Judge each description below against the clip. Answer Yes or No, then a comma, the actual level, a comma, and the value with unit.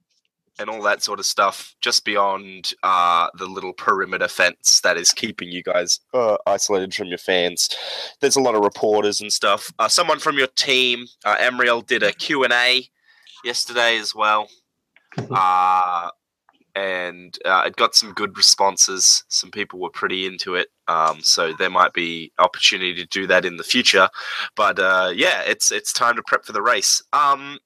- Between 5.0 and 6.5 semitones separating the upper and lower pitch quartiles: Yes, average, 5.3 semitones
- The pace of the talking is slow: No, average, 175 wpm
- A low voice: Yes, low, 105 Hz